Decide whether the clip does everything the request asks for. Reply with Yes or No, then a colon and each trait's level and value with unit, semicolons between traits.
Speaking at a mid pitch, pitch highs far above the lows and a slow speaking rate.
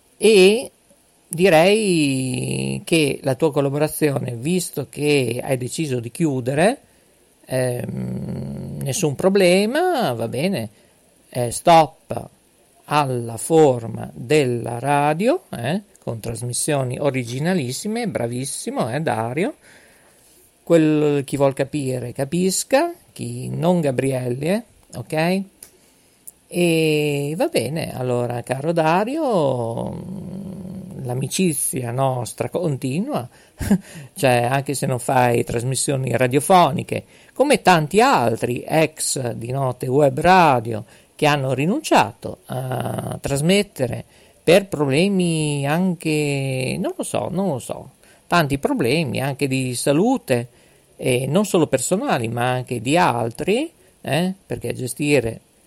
Yes: medium, 145 Hz; wide, 5.9 semitones; slow, 100 wpm